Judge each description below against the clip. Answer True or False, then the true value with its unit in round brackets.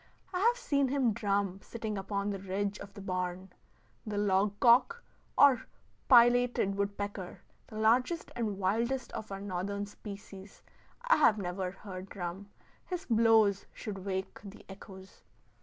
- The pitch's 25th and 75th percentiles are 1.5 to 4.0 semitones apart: True (3.3 semitones)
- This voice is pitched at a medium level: False (205 Hz)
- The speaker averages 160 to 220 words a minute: False (140 wpm)